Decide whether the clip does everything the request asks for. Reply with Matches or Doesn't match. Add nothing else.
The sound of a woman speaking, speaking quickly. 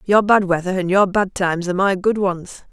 Matches